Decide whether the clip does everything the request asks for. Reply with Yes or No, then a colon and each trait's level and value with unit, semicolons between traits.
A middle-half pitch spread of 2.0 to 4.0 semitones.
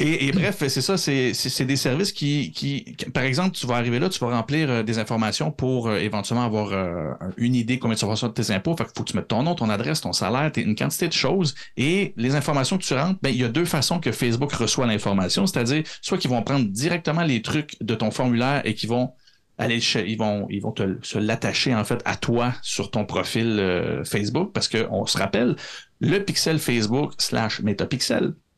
No: average, 4.7 semitones